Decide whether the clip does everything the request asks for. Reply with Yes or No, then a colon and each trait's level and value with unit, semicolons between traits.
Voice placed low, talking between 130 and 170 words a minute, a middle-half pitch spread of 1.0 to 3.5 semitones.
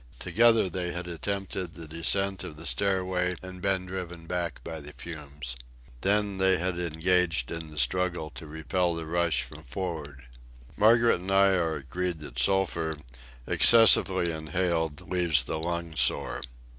Yes: very low, 85 Hz; average, 150 wpm; average, 2.8 semitones